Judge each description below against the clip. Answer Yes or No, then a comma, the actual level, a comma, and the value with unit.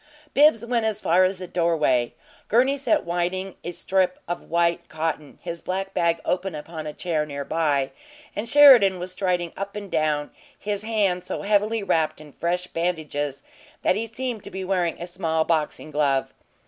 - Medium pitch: Yes, medium, 180 Hz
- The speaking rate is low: No, average, 175 wpm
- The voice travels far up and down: No, average, 3.9 semitones